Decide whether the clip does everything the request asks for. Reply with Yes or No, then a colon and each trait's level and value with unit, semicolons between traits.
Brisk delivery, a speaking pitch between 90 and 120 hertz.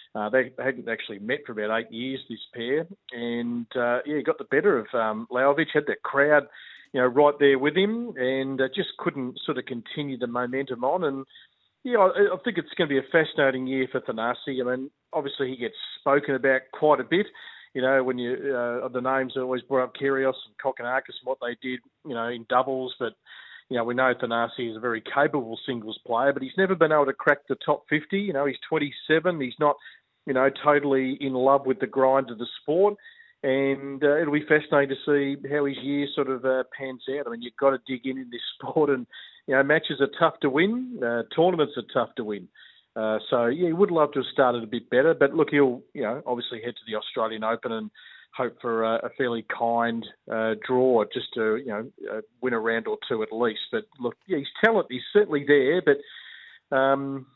No: fast, 230 wpm; low, 135 Hz